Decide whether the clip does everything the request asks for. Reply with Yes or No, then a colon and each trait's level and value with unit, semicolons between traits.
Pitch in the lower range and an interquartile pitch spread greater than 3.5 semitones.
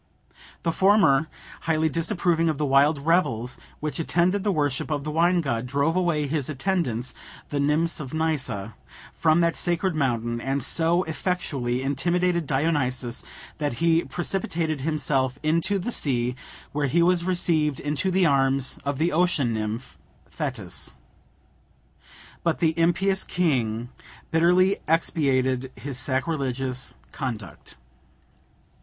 No: medium, 155 Hz; average, 4.3 semitones